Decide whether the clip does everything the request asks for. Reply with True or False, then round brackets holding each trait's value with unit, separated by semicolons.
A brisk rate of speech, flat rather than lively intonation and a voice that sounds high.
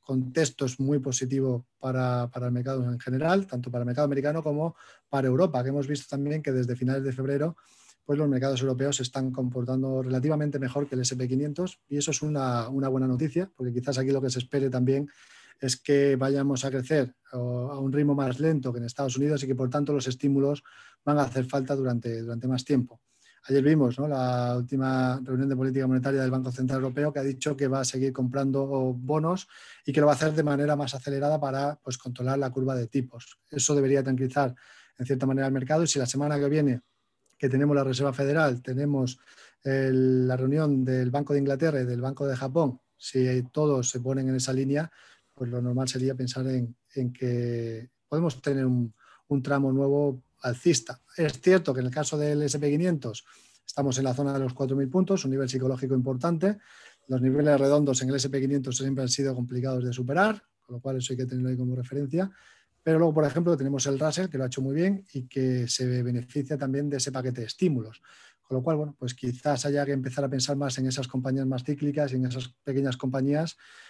False (215 wpm; 1.9 semitones; 135 Hz)